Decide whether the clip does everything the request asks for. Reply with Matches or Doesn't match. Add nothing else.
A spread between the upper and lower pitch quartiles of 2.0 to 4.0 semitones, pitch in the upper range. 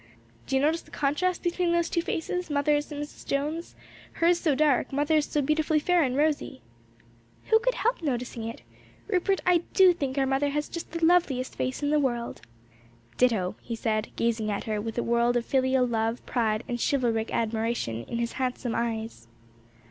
Doesn't match